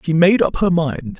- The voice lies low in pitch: No, medium, 165 Hz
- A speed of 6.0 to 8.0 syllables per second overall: No, 4.7 syllables/s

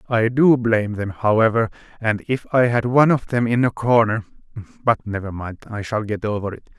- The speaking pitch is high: No, low, 115 Hz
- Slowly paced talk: No, average, 195 wpm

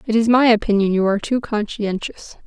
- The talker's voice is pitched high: Yes, high, 215 Hz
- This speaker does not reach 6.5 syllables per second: Yes, 5.7 syllables/s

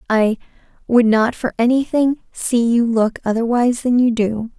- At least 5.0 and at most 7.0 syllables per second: No, 4.7 syllables/s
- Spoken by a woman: Yes, female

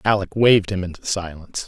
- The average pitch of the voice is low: Yes, very low, 95 Hz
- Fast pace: No, average, 180 wpm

